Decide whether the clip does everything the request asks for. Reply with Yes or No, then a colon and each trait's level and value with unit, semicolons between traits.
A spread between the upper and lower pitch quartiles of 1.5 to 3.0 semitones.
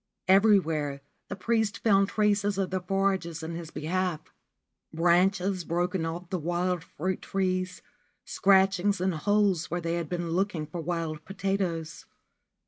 Yes: average, 2.7 semitones